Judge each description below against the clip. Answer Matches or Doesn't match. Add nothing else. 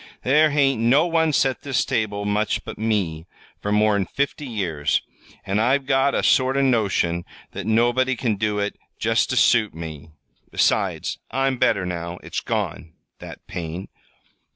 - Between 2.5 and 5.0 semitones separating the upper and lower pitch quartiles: Doesn't match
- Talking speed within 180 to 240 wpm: Doesn't match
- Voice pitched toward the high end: Doesn't match